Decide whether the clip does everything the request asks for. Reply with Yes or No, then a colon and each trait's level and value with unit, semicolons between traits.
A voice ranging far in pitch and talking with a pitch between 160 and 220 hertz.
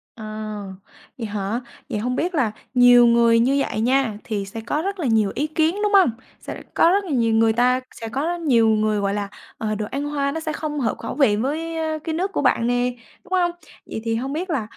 No: wide, 5.8 semitones; very high, 250 Hz